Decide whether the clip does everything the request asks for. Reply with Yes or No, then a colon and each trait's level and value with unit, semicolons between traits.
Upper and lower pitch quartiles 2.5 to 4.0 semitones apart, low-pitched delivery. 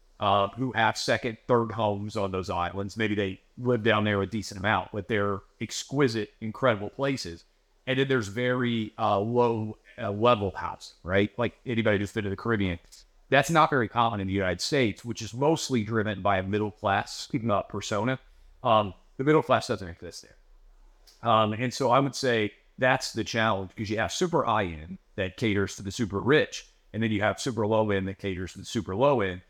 Yes: average, 3.5 semitones; low, 110 Hz